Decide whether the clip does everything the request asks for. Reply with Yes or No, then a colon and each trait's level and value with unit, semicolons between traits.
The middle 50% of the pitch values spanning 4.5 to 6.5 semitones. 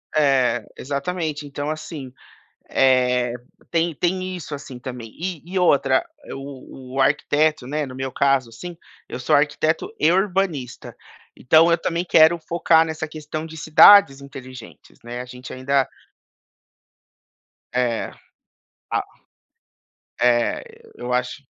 No: average, 4.0 semitones